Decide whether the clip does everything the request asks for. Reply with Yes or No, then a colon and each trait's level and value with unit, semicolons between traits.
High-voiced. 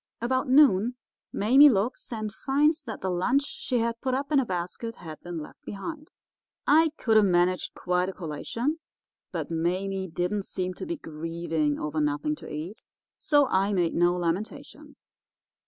Yes: high, 195 Hz